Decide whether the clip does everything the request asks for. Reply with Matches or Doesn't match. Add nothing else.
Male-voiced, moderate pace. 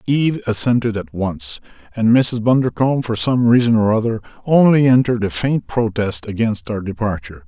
Matches